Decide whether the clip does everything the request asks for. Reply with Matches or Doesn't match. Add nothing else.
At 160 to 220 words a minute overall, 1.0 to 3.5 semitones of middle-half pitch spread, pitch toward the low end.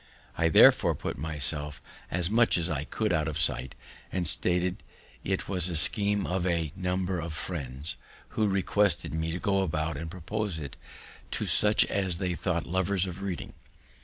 Matches